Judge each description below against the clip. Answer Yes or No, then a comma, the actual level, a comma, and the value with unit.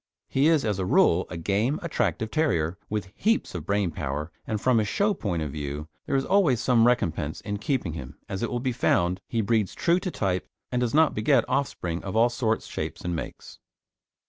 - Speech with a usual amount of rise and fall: No, wide, 6.6 semitones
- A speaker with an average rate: No, fast, 210 wpm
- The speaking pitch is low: Yes, low, 105 Hz